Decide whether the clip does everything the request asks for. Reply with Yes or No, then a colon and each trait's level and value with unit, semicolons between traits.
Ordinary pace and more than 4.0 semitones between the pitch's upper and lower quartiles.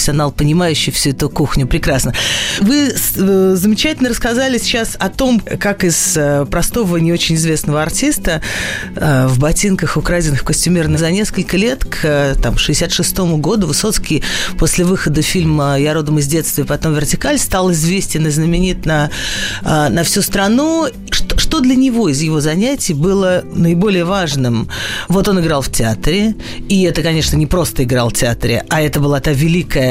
Yes: average, 150 wpm; average, 4.4 semitones